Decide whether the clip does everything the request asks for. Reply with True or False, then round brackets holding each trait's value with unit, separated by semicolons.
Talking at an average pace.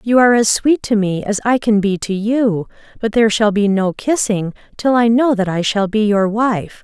False (235 wpm)